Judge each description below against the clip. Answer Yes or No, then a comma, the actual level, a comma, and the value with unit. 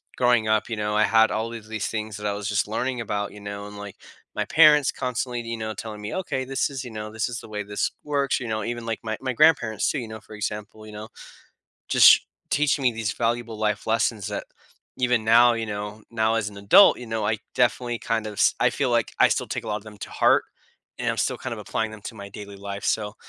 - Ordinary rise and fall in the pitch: No, narrow, 2.2 semitones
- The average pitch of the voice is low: Yes, low, 110 Hz